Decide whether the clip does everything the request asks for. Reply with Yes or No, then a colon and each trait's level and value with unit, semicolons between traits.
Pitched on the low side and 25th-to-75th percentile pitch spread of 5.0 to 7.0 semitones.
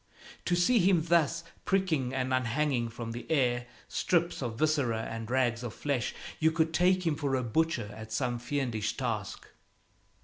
Yes: low, 130 Hz; average, 5.3 semitones